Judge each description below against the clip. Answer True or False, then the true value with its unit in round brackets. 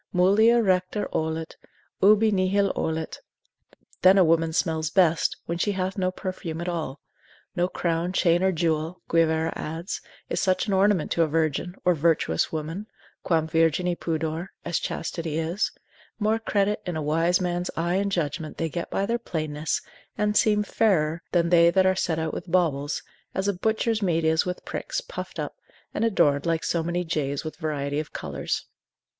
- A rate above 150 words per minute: True (175 wpm)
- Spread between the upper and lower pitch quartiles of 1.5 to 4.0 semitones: True (2.9 semitones)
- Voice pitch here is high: False (170 Hz)